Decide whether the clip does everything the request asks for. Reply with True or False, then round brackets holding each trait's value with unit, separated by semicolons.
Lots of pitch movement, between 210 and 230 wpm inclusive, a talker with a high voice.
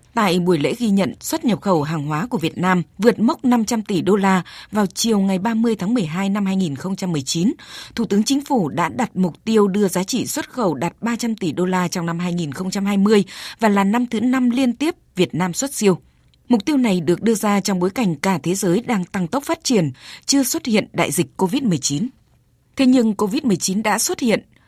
False (4.8 semitones; 215 wpm; 200 Hz)